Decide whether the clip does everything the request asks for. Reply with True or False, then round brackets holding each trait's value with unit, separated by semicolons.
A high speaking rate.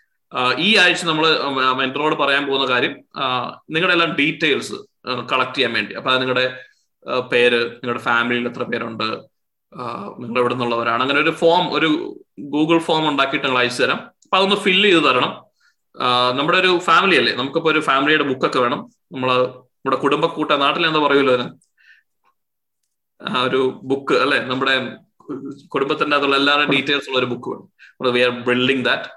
True (140 wpm)